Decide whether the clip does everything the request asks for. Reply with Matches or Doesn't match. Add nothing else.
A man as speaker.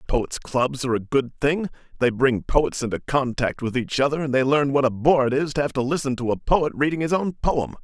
Matches